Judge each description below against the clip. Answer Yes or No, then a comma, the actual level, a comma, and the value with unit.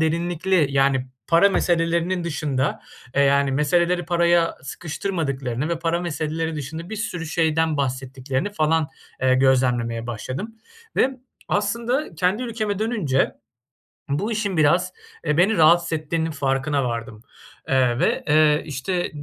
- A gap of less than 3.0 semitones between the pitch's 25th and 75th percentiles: No, average, 4.4 semitones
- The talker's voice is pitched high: No, medium, 160 Hz